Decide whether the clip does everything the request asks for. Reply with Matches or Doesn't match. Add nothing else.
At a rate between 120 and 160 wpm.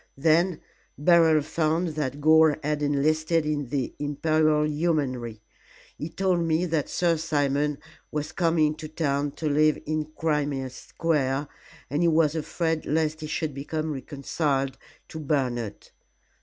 Matches